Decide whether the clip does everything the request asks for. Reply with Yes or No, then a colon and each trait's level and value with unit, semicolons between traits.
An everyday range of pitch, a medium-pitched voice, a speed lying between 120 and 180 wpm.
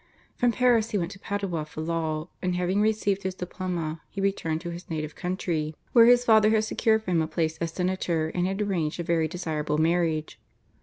No: average, 3.9 semitones; medium, 180 Hz; fast, 205 wpm